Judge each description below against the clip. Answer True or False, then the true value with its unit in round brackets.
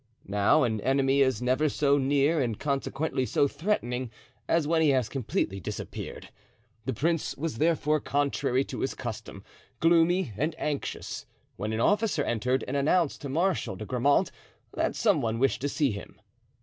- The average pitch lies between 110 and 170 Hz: True (140 Hz)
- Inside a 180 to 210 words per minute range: False (160 wpm)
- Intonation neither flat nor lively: True (3.7 semitones)